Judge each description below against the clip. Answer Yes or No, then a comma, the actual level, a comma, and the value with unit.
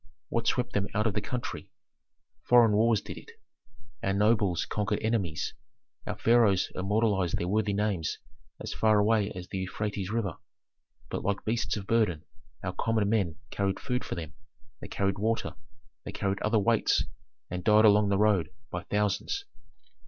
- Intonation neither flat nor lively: No, narrow, 2.3 semitones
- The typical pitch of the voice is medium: No, low, 105 Hz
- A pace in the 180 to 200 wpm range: No, average, 160 wpm